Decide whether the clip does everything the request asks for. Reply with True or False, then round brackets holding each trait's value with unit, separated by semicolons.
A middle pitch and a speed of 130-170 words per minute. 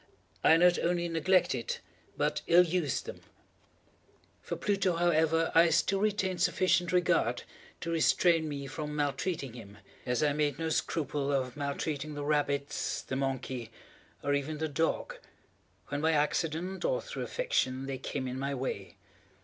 True (155 Hz; 150 wpm)